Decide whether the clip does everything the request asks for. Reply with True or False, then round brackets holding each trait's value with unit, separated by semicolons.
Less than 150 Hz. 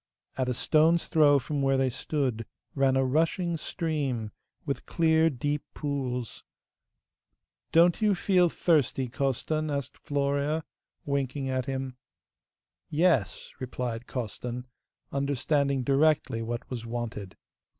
True (140 Hz)